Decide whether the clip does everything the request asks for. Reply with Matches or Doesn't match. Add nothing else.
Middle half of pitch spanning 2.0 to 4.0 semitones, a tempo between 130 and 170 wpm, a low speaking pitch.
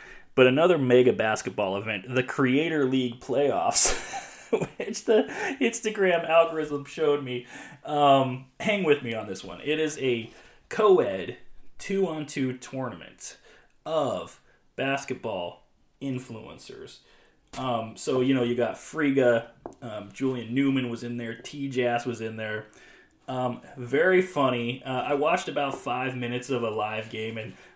Matches